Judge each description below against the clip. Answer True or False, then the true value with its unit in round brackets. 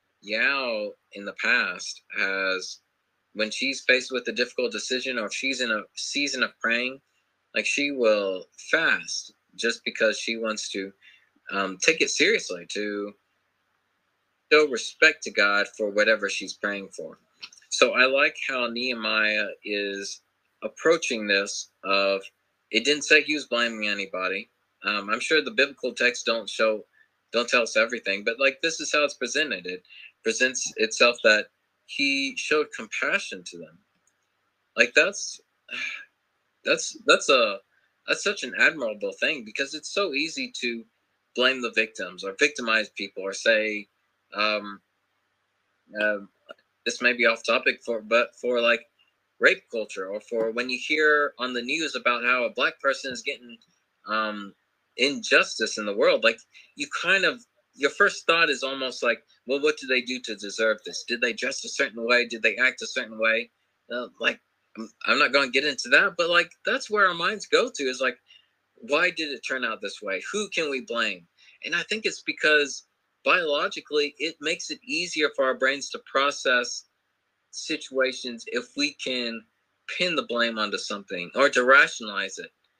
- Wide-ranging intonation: True (6.1 semitones)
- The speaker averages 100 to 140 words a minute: False (170 wpm)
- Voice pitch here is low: True (120 Hz)